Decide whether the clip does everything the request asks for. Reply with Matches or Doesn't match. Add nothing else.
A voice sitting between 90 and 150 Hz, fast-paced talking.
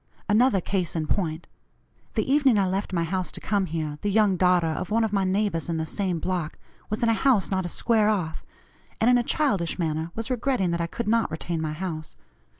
Doesn't match